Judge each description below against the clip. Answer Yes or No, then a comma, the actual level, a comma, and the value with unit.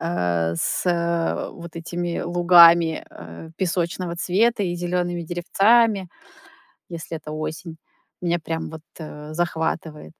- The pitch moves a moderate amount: No, narrow, 1.5 semitones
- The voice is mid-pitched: Yes, medium, 170 Hz